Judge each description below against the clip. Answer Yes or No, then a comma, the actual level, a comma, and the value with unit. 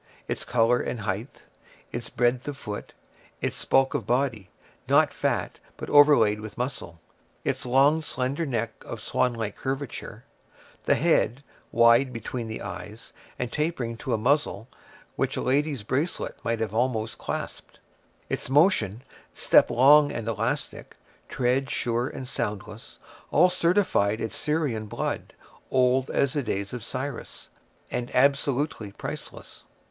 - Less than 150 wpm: Yes, slow, 135 wpm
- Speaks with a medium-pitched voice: No, low, 125 Hz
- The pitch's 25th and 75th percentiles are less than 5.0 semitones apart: Yes, average, 3.7 semitones